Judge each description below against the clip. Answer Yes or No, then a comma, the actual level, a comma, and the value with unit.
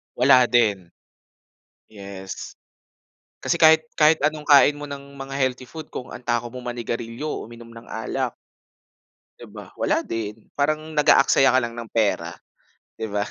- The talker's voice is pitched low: Yes, low, 125 Hz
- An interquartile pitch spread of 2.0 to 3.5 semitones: No, average, 4.1 semitones